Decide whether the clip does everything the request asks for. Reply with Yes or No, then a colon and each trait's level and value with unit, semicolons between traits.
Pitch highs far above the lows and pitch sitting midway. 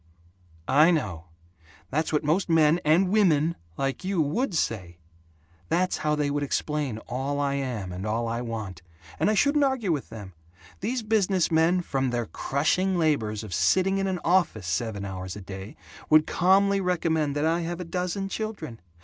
Yes: wide, 7.7 semitones; medium, 155 Hz